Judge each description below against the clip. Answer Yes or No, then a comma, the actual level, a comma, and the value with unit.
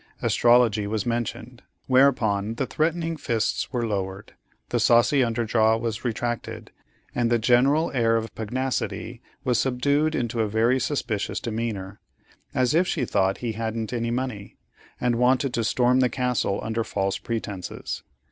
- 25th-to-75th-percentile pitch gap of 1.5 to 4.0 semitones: Yes, narrow, 2.4 semitones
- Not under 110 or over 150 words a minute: Yes, average, 145 wpm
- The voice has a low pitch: Yes, low, 120 Hz